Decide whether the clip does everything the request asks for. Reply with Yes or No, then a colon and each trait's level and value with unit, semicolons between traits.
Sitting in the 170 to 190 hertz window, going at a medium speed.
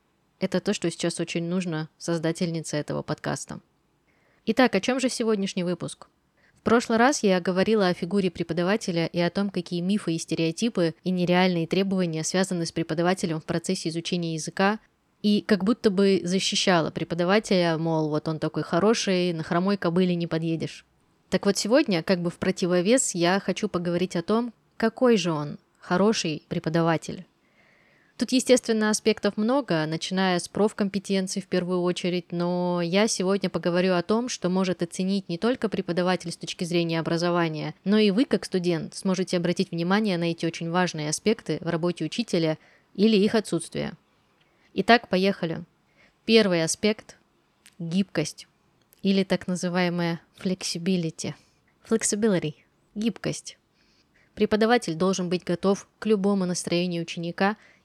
Yes: medium, 185 Hz; average, 140 wpm